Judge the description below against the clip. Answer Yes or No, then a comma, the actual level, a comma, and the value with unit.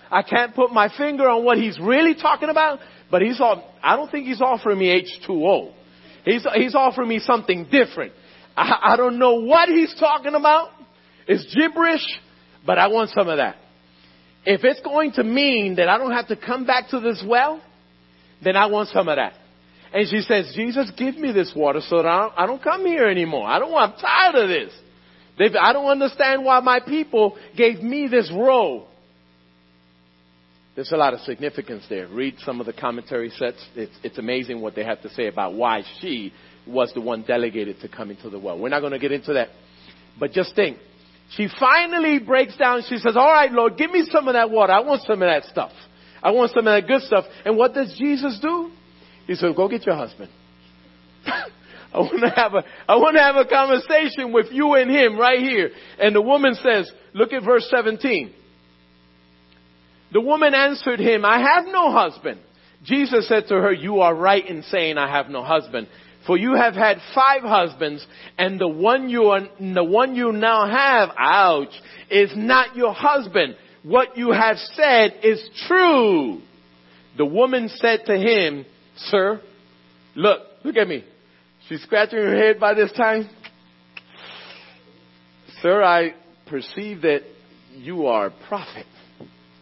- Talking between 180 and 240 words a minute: Yes, average, 185 wpm